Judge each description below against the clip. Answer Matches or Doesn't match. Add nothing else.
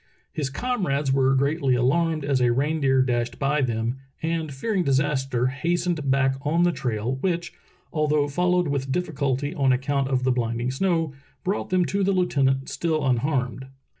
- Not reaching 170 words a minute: Matches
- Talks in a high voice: Doesn't match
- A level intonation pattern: Doesn't match